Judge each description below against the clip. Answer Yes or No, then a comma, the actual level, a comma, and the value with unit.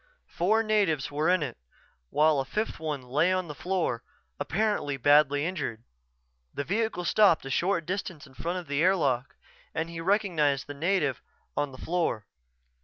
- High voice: No, medium, 160 Hz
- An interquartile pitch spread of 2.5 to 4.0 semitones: No, average, 4.5 semitones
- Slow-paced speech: No, average, 165 wpm